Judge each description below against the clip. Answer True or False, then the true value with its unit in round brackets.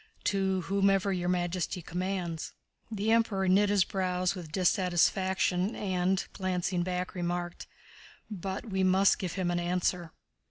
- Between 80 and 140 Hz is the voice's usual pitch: False (185 Hz)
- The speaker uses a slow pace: True (130 wpm)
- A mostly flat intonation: True (1.5 semitones)